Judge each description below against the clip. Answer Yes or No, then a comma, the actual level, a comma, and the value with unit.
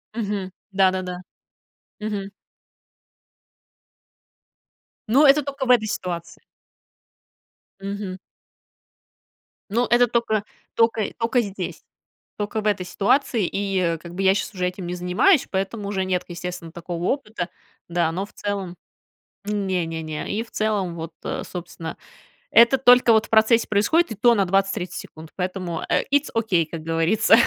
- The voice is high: Yes, high, 195 Hz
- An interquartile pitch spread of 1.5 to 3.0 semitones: No, average, 3.7 semitones